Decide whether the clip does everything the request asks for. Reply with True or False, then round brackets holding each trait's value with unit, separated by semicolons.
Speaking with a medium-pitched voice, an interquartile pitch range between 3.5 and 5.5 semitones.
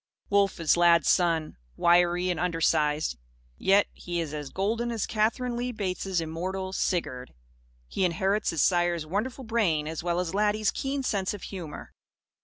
True (180 Hz; 3.8 semitones)